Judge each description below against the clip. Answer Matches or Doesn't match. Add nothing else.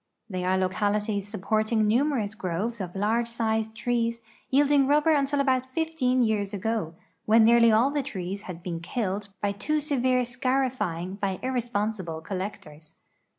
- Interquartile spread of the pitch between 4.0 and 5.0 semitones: Matches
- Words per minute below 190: Matches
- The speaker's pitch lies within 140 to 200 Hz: Doesn't match